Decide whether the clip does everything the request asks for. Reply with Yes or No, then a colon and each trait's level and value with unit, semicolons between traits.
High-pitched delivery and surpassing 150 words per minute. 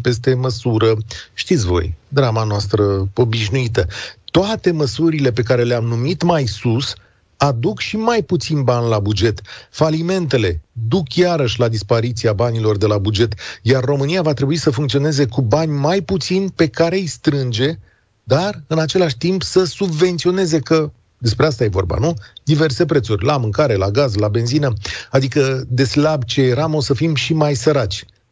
No: low, 135 Hz; average, 160 wpm